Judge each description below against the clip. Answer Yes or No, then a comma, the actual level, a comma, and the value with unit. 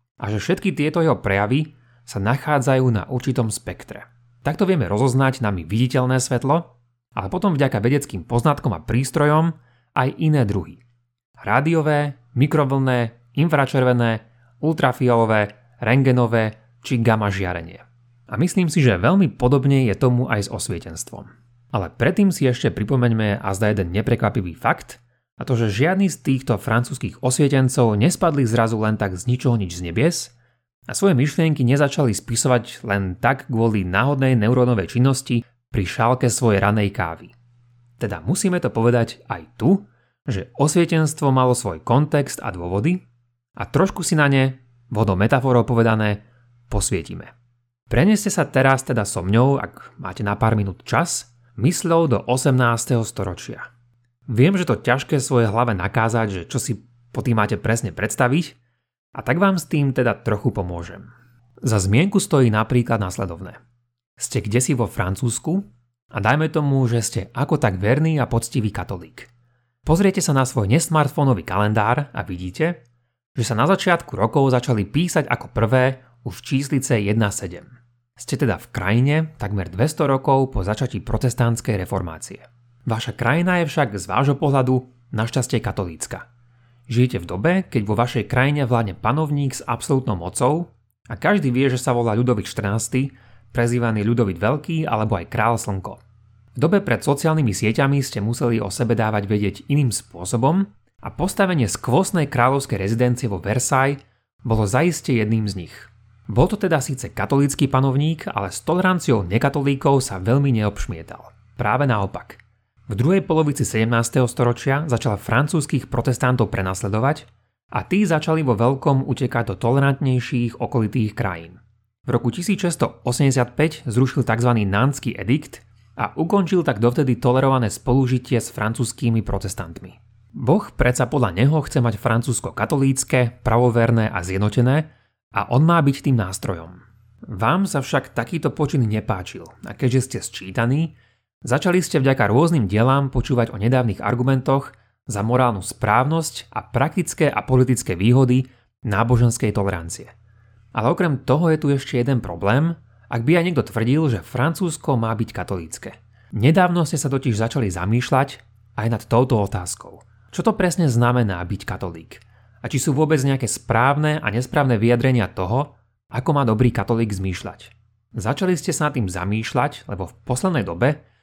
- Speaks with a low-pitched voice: Yes, low, 120 Hz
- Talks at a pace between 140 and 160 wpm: Yes, average, 145 wpm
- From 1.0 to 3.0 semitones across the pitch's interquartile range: No, average, 3.6 semitones